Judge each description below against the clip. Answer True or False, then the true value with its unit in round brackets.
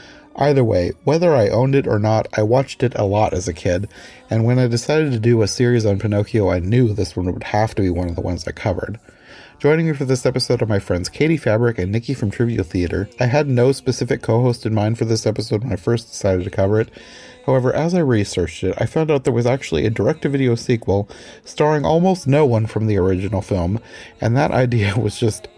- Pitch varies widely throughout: False (4.1 semitones)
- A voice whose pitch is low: True (115 Hz)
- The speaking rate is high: True (240 wpm)